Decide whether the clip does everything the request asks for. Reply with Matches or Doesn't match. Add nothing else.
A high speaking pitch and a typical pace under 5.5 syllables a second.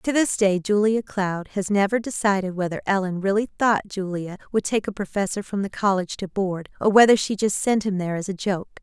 Doesn't match